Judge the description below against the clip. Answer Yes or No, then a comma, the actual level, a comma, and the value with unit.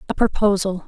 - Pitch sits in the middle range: No, high, 195 Hz